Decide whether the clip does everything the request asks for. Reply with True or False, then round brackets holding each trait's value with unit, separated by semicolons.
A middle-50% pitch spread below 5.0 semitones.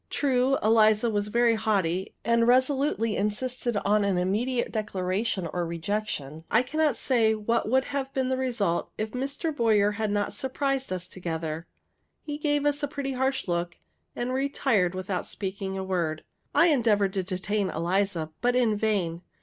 False (5.4 semitones)